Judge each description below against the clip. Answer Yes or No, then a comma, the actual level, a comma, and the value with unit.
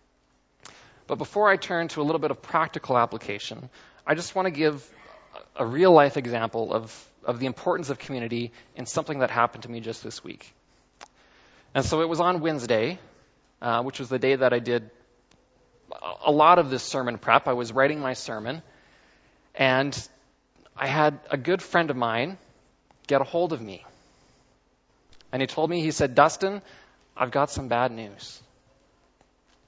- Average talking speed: Yes, average, 170 wpm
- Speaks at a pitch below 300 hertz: Yes, low, 135 Hz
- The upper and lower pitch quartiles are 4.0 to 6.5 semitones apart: Yes, average, 4.9 semitones